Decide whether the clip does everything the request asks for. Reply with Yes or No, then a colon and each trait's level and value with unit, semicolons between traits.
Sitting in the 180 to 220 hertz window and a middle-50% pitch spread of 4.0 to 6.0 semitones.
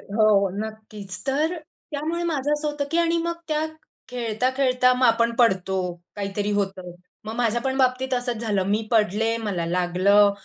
No: high, 230 Hz; average, 4.6 semitones